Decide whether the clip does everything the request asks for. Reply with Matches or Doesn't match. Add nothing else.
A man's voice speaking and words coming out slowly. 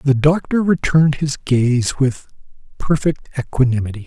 Matches